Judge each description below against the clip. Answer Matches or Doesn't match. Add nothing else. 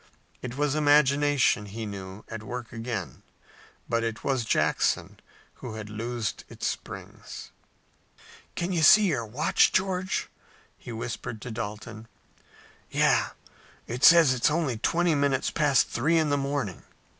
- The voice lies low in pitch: Matches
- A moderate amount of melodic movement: Matches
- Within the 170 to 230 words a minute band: Doesn't match